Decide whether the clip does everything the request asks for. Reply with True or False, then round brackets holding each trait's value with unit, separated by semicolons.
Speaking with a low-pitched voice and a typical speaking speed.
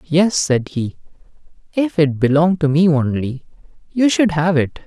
False (160 Hz; 160 wpm)